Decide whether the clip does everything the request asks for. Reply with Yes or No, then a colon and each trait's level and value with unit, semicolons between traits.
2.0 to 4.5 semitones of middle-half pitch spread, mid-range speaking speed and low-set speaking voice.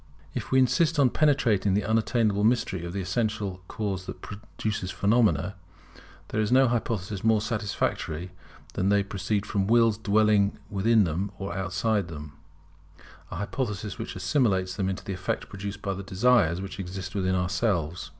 Yes: average, 3.0 semitones; average, 160 wpm; low, 100 Hz